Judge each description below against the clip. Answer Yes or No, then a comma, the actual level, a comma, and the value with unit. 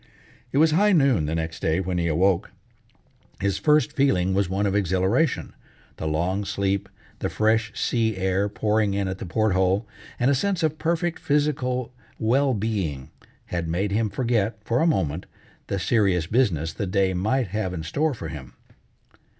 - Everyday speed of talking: Yes, average, 175 wpm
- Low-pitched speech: Yes, low, 100 Hz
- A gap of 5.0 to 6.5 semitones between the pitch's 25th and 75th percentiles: Yes, wide, 5.4 semitones